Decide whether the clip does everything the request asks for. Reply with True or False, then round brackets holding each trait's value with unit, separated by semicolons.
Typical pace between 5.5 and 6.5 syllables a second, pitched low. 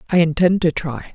False (5.8 syllables/s; 165 Hz)